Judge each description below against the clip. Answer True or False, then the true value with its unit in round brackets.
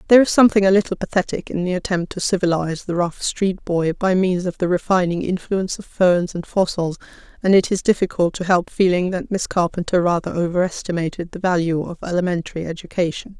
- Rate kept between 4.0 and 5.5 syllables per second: False (6.0 syllables/s)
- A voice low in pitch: False (180 Hz)